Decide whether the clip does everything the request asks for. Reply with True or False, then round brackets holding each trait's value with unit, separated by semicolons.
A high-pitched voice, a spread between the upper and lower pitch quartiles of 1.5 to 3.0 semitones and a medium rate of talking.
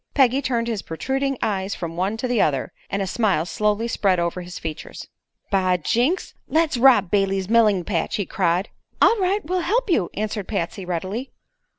False (205 Hz; 5.6 semitones; 180 wpm)